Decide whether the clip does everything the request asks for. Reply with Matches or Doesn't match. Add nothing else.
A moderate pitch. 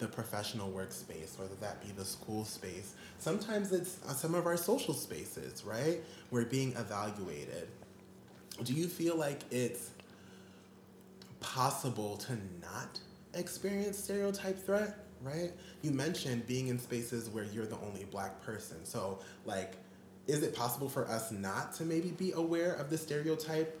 Doesn't match